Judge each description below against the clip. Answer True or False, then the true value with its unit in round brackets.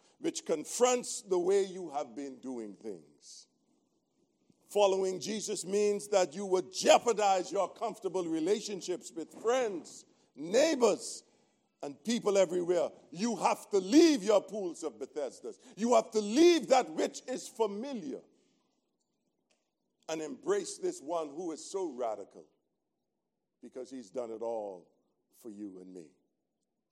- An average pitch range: False (7.6 semitones)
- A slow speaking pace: True (130 wpm)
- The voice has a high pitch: True (205 Hz)